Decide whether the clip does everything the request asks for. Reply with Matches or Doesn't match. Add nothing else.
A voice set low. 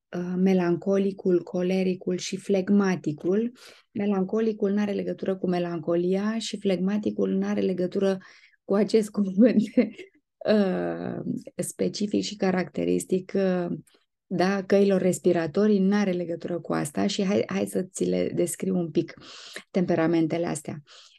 Doesn't match